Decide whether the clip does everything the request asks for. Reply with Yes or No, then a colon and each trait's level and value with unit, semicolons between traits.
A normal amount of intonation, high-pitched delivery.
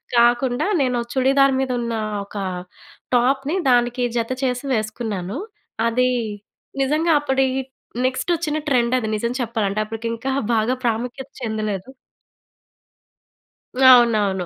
Yes: average, 3.0 semitones; high, 245 Hz